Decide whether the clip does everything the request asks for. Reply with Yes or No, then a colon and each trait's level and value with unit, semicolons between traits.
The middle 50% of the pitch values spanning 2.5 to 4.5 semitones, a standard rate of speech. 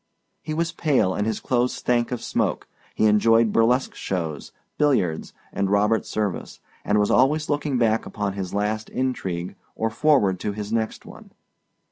Yes: average, 3.9 semitones; average, 160 wpm